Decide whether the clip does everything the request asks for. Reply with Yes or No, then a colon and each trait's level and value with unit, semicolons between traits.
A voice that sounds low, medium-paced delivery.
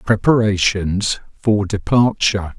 No: low, 100 Hz; slow, 70 wpm